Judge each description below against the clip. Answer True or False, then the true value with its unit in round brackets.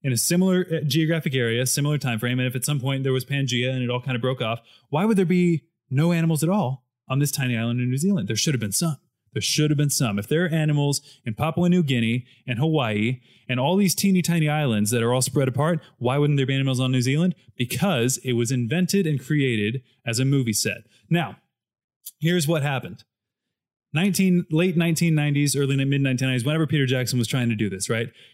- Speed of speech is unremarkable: False (225 wpm)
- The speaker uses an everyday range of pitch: True (4.5 semitones)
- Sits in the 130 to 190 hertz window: True (135 Hz)